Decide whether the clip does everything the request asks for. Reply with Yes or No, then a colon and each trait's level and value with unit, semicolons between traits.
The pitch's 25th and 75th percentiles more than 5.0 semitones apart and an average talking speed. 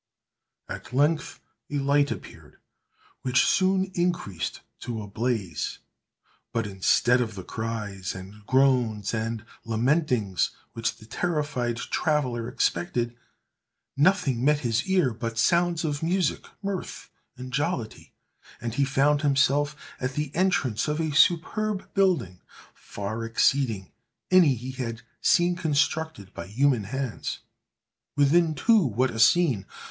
No: wide, 5.5 semitones; slow, 125 wpm